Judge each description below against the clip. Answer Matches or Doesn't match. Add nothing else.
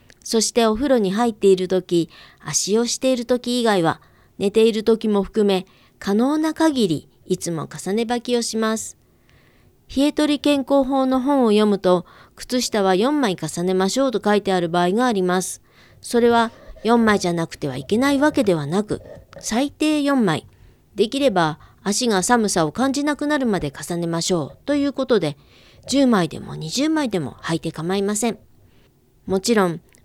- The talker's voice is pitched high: Matches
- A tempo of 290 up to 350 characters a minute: Matches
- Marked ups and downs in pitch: Matches